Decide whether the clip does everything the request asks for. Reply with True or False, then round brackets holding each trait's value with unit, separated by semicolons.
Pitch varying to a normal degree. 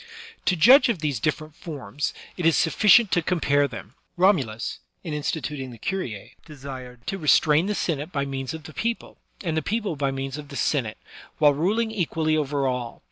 True (4.4 semitones)